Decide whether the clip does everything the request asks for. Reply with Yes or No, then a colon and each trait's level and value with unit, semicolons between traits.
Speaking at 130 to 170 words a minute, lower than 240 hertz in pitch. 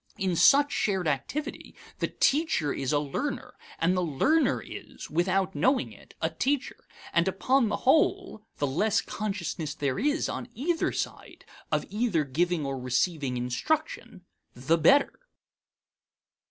Yes: average, 140 wpm; high, 190 Hz